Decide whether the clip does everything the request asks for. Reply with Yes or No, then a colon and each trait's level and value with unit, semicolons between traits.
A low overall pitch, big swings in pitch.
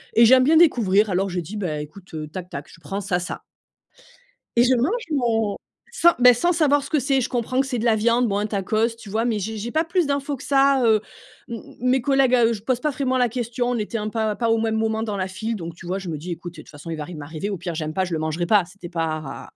No: high, 220 Hz; wide, 5.8 semitones